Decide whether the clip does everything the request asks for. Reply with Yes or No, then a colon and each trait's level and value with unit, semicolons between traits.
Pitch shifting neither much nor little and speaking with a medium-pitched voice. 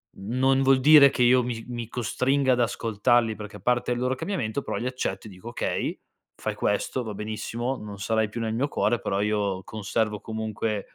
No: average, 3.0 semitones; low, 115 Hz